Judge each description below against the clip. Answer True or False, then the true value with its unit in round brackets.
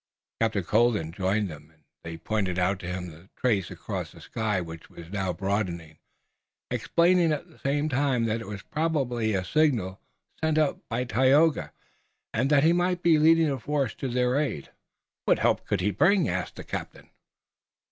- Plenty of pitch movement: True (8.0 semitones)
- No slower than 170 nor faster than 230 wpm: True (175 wpm)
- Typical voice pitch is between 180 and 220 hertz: False (115 Hz)